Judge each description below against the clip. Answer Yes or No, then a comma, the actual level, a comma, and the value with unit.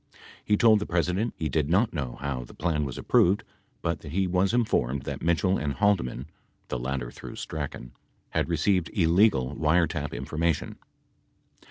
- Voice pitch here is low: Yes, very low, 80 Hz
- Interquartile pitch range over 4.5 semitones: Yes, average, 5.1 semitones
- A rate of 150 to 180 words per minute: Yes, average, 170 wpm